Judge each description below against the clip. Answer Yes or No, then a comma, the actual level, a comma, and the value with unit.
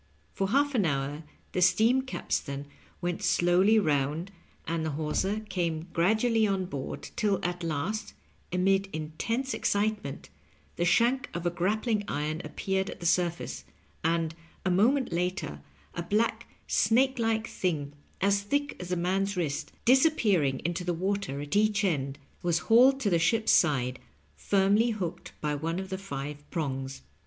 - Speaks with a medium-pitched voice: Yes, medium, 180 Hz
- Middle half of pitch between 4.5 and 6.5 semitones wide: Yes, average, 5.2 semitones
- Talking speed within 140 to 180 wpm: Yes, average, 150 wpm